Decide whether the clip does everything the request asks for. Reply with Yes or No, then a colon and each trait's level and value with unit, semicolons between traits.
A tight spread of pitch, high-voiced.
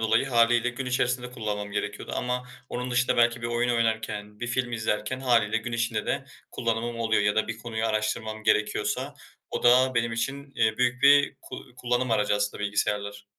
No: narrow, 2.3 semitones; low, 115 Hz